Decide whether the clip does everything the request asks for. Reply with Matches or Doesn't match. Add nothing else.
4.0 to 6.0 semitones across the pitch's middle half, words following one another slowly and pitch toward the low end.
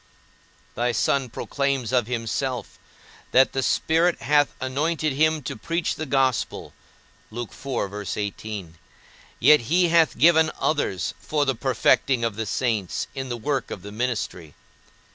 Matches